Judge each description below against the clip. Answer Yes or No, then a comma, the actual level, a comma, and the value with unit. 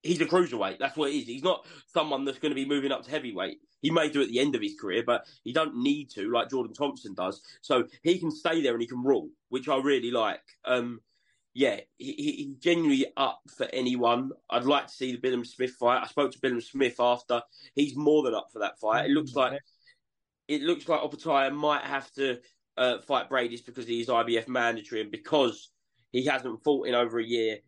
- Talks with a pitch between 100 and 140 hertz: Yes, low, 135 Hz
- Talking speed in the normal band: No, fast, 230 wpm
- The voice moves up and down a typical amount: Yes, average, 4.1 semitones